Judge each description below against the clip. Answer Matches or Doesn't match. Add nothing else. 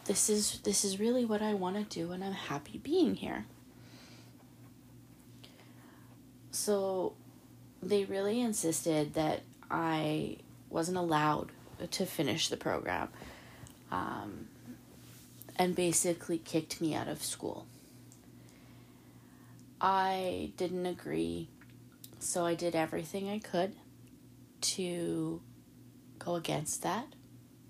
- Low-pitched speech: Doesn't match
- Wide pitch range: Matches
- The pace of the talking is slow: Matches